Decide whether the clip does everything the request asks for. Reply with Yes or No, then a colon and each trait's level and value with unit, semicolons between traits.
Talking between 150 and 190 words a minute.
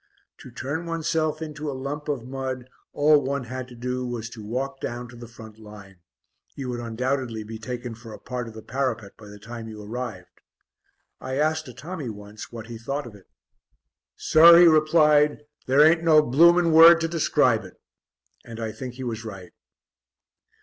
Yes: average, 185 wpm